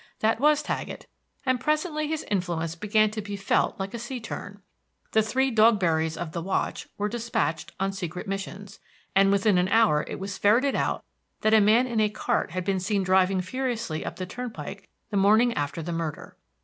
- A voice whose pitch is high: Yes, high, 205 Hz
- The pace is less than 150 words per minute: No, average, 190 wpm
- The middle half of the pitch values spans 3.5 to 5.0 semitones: Yes, average, 3.9 semitones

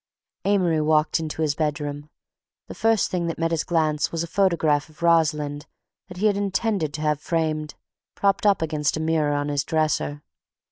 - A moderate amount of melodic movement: No, narrow, 2.3 semitones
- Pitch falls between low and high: Yes, medium, 160 Hz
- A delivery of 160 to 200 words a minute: Yes, average, 180 wpm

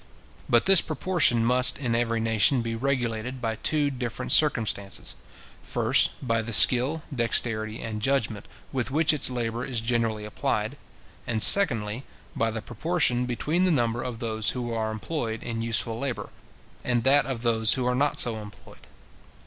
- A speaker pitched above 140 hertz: No, low, 120 Hz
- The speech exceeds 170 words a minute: No, average, 160 wpm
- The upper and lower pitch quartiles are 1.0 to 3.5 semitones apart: Yes, average, 2.8 semitones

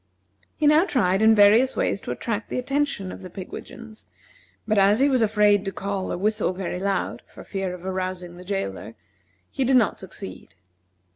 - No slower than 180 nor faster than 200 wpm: Yes, average, 185 wpm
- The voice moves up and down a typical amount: Yes, average, 3.4 semitones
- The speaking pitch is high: Yes, high, 200 Hz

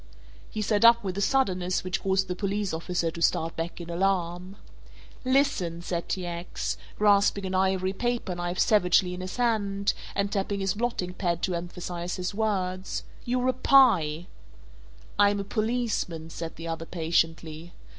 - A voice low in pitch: No, medium, 185 Hz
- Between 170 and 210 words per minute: No, average, 155 wpm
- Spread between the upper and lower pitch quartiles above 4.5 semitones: No, average, 3.0 semitones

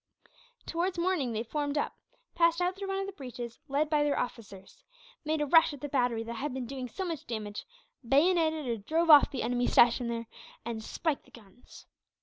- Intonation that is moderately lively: No, wide, 5.7 semitones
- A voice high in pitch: Yes, very high, 280 Hz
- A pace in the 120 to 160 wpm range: No, average, 200 wpm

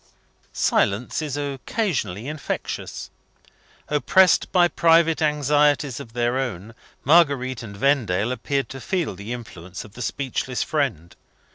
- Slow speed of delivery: Yes, slow, 120 wpm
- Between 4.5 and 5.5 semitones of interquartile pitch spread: Yes, average, 4.9 semitones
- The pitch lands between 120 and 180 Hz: Yes, low, 135 Hz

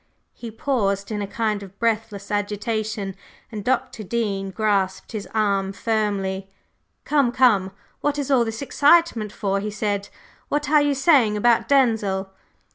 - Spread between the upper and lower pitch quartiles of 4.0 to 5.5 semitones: No, average, 3.3 semitones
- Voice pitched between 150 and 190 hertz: No, high, 215 Hz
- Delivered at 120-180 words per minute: Yes, average, 145 wpm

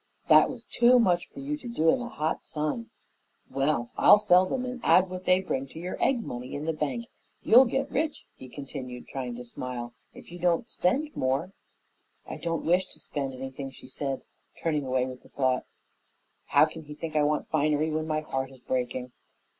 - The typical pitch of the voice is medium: Yes, medium, 155 Hz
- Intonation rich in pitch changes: Yes, wide, 5.8 semitones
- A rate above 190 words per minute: Yes, average, 200 wpm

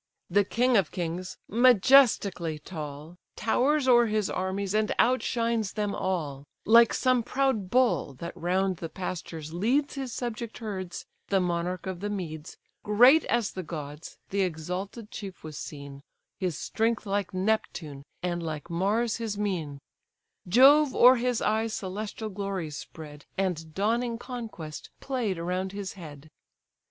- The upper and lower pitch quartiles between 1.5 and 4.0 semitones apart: No, average, 5.3 semitones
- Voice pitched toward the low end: No, high, 195 Hz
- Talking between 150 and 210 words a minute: No, average, 140 wpm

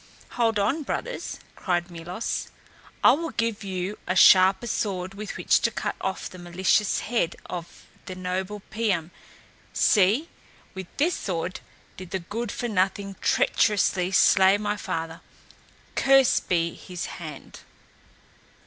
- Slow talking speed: Yes, slow, 130 wpm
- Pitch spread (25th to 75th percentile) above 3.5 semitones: No, average, 3.0 semitones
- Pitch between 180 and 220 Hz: Yes, high, 190 Hz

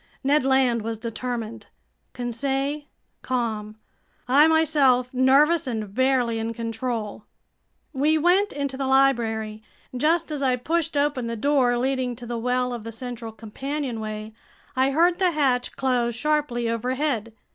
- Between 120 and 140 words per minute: Yes, slow, 135 wpm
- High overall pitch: Yes, very high, 255 Hz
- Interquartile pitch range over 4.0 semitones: No, average, 3.6 semitones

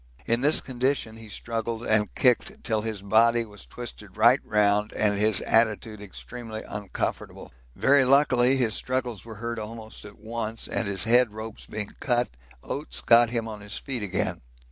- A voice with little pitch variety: Yes, narrow, 2.3 semitones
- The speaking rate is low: No, average, 165 wpm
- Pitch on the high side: No, low, 115 Hz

